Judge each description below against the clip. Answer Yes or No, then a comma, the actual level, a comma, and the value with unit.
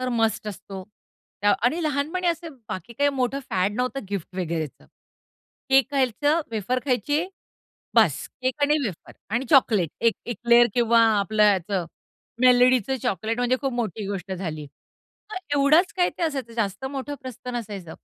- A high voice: Yes, high, 240 Hz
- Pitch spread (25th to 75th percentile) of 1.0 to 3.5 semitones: No, average, 5.2 semitones